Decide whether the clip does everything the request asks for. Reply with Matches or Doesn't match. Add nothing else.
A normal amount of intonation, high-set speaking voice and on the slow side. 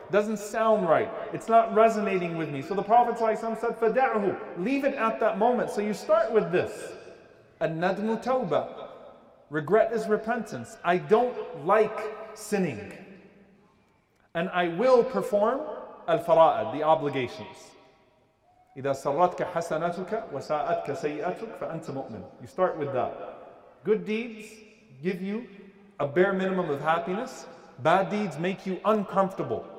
Matches